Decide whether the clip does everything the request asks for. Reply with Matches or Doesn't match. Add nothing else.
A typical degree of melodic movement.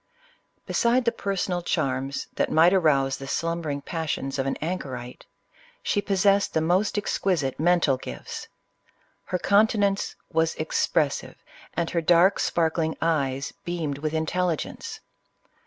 Matches